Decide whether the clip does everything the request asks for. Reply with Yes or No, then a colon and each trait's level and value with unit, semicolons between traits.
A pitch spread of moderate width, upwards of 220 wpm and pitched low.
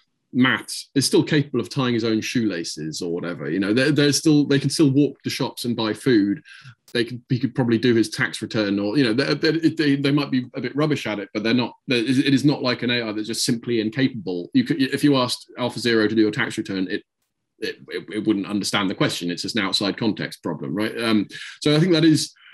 Yes: average, 4.4 semitones; fast, 250 wpm; low, 125 Hz